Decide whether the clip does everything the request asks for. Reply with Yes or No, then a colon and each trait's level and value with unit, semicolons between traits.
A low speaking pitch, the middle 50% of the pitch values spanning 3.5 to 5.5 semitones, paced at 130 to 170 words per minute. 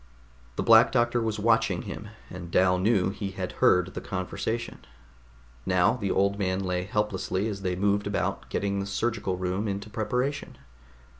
No: low, 100 Hz; average, 2.7 semitones; average, 160 wpm